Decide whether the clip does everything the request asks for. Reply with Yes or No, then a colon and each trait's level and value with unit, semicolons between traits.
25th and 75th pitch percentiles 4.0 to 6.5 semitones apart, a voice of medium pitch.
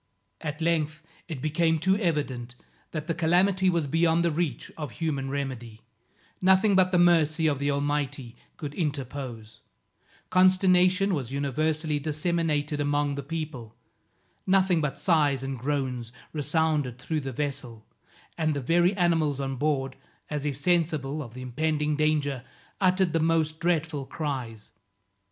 No: average, 3.3 semitones; medium, 150 Hz